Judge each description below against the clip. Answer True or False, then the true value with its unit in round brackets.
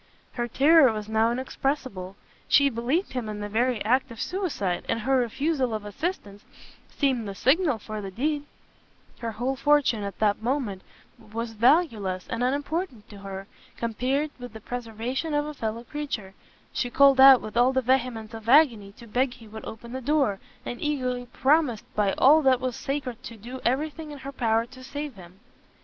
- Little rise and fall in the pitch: False (4.0 semitones)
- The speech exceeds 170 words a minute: True (180 wpm)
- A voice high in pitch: True (245 Hz)